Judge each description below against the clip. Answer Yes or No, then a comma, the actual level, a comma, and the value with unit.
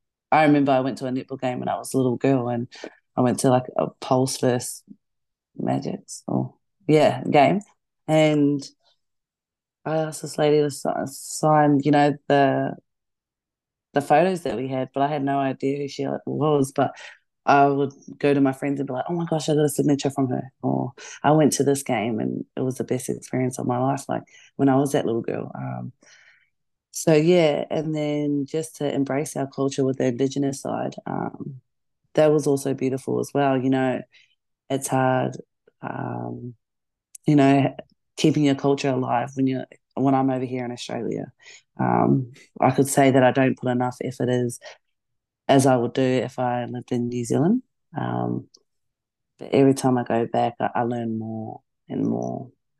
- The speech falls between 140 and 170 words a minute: No, average, 185 wpm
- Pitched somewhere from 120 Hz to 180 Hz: Yes, low, 135 Hz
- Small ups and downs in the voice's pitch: Yes, narrow, 2.3 semitones